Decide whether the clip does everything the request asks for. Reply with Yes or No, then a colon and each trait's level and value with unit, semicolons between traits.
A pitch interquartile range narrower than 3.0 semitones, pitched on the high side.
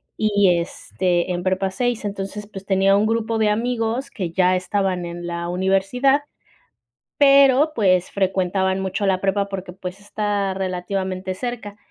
Yes: narrow, 2.5 semitones; high, 195 Hz